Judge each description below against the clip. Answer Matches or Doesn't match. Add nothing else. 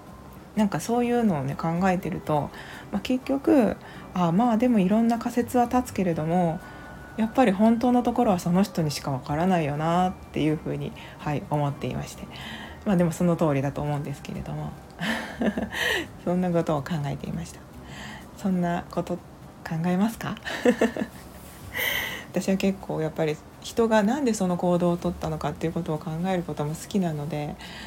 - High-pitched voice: Doesn't match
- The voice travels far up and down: Matches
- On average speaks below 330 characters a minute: Doesn't match